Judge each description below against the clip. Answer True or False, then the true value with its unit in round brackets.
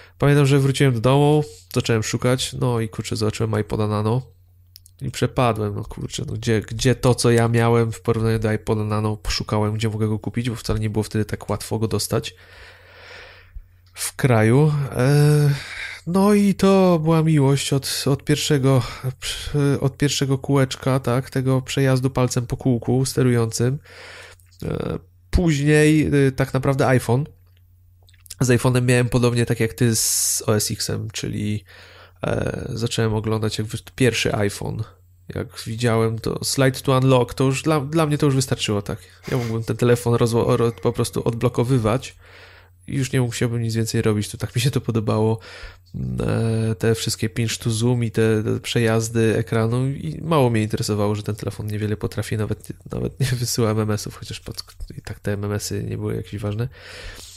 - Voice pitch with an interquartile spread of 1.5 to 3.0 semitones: False (3.7 semitones)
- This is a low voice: True (115 Hz)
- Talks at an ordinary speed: False (165 wpm)